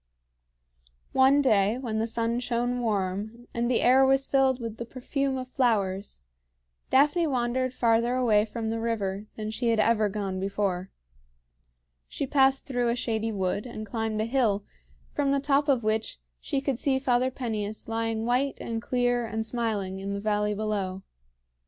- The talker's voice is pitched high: Yes, high, 230 Hz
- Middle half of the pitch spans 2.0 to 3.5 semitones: Yes, average, 3.2 semitones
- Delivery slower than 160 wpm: No, average, 165 wpm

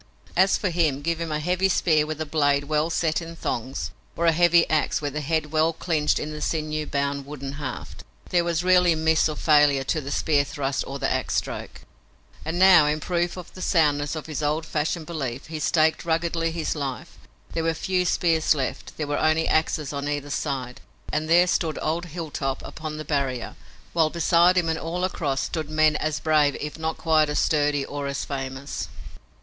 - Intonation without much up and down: Yes, narrow, 2.3 semitones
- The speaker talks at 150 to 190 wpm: No, average, 200 wpm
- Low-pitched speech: No, medium, 155 Hz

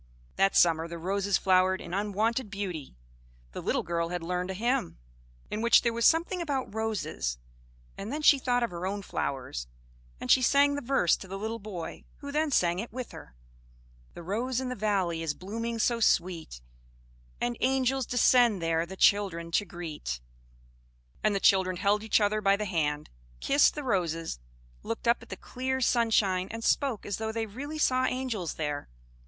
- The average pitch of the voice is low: No, high, 205 Hz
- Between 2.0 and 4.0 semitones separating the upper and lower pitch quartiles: No, wide, 5.5 semitones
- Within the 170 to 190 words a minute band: Yes, average, 180 wpm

